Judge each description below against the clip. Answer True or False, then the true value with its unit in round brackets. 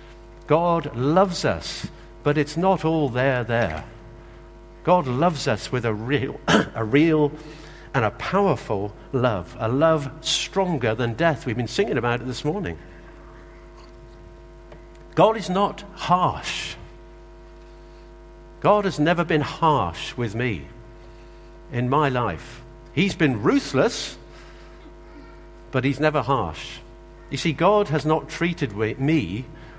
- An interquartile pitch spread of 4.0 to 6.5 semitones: True (5.4 semitones)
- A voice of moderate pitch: True (145 Hz)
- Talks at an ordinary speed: False (125 wpm)